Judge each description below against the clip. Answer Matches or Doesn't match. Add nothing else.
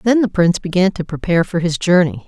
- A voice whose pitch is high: Doesn't match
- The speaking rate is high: Matches